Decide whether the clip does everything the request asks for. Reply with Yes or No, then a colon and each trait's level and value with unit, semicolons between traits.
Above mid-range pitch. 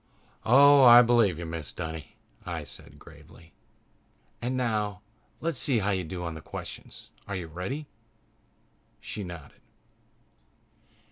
No: low, 100 Hz